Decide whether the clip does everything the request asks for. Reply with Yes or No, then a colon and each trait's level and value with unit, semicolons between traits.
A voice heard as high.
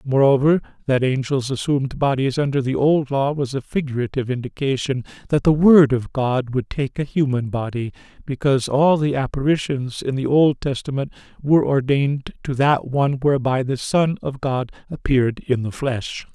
No: low, 135 Hz